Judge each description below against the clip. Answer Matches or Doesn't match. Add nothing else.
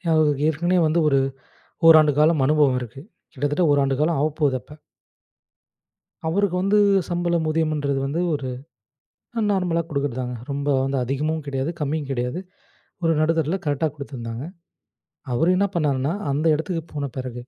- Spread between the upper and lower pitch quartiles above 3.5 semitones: Doesn't match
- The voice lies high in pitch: Doesn't match